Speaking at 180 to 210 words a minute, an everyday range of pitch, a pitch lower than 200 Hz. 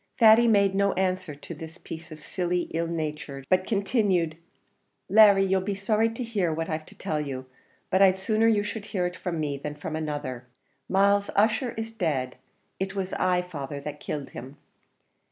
Yes: average, 185 wpm; average, 4.7 semitones; medium, 185 Hz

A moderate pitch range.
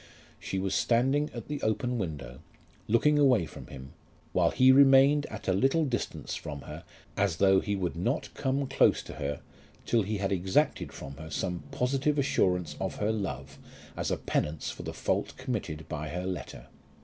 No: wide, 7.3 semitones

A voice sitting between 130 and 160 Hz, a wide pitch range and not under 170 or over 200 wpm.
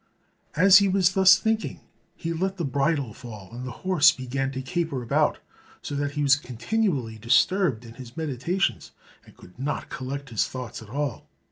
Yes: medium, 140 Hz; wide, 6.2 semitones; average, 175 wpm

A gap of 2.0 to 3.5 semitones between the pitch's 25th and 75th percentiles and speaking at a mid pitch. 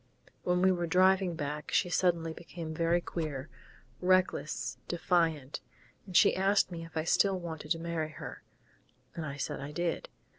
Yes: narrow, 2.4 semitones; medium, 170 Hz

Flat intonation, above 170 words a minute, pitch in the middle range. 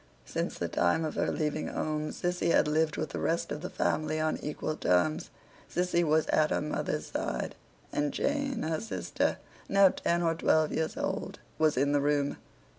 Yes: narrow, 2.1 semitones; average, 185 wpm; medium, 155 Hz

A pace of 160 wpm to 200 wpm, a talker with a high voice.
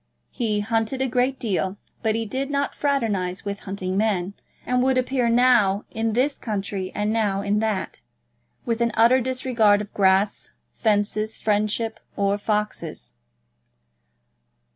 No: average, 140 wpm; high, 215 Hz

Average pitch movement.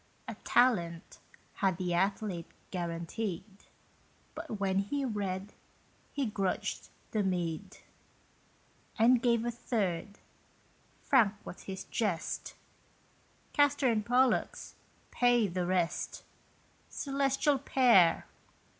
Yes: average, 4.9 semitones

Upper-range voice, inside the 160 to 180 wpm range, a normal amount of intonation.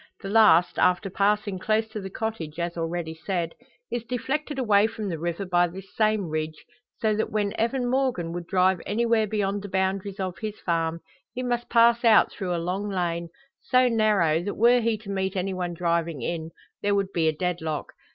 No: high, 195 Hz; average, 195 wpm; average, 4.1 semitones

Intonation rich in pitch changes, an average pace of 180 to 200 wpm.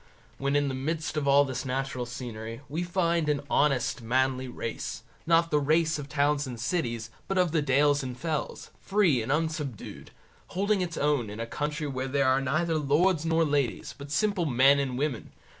No: average, 3.7 semitones; average, 190 wpm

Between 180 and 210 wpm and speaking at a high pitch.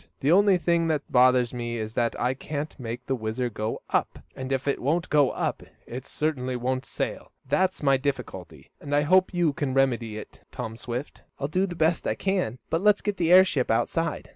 No: fast, 205 wpm; low, 135 Hz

